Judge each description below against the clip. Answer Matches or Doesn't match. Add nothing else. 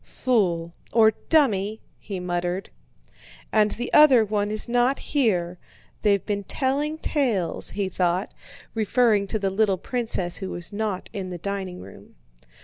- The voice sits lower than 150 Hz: Doesn't match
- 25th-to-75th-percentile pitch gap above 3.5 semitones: Matches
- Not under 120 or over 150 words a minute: Matches